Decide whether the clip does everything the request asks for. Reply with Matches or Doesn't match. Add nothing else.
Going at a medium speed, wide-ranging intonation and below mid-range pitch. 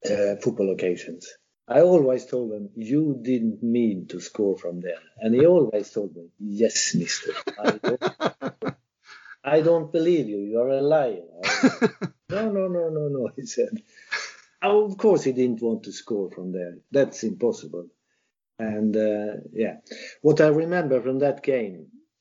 Matches